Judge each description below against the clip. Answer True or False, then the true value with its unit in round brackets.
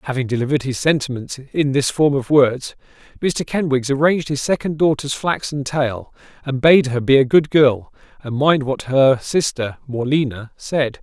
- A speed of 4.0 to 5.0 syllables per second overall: True (4.8 syllables/s)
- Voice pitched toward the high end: False (135 Hz)